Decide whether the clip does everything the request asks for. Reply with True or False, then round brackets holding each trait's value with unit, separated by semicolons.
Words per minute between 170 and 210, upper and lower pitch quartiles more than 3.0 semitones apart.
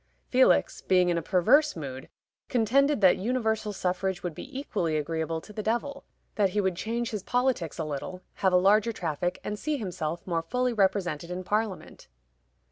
True (175 wpm; 4.6 semitones)